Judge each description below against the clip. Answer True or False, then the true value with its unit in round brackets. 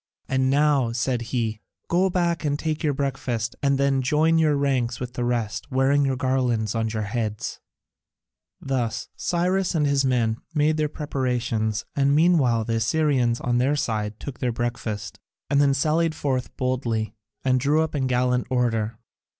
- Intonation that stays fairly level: False (3.6 semitones)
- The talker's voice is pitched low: True (130 Hz)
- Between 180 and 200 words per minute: False (165 wpm)